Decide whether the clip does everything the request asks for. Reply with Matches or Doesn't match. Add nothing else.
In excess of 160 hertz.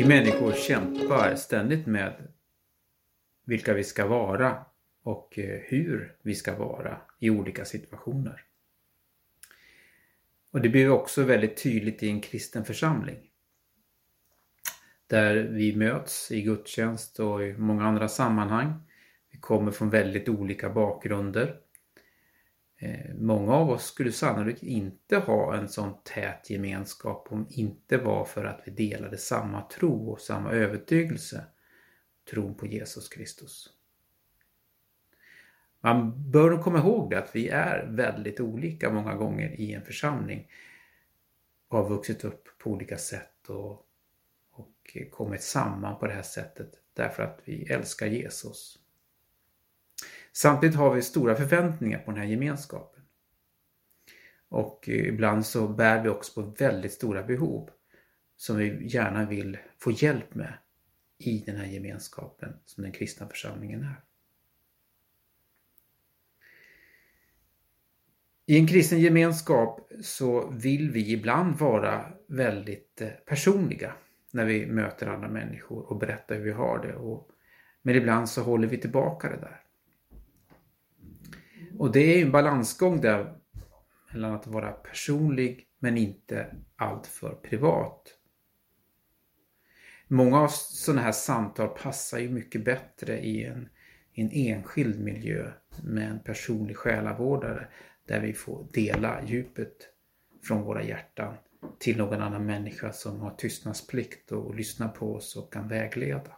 Doesn't match